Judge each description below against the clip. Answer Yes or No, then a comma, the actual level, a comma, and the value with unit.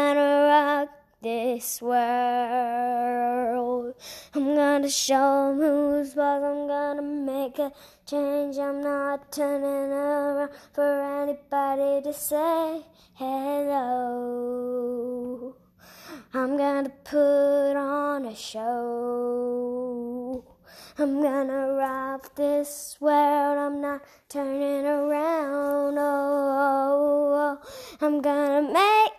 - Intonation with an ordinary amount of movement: No, narrow, 1.9 semitones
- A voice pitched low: No, very high, 280 Hz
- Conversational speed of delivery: No, slow, 95 wpm